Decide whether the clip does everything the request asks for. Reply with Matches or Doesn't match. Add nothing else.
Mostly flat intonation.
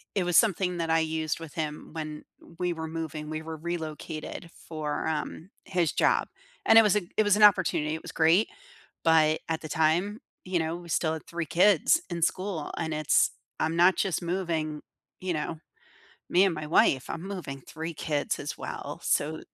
Matches